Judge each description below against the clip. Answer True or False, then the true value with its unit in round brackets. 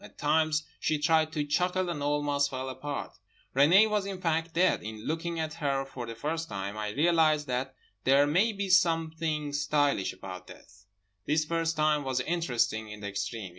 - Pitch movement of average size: True (3.9 semitones)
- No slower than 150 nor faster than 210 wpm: True (180 wpm)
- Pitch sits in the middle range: True (150 Hz)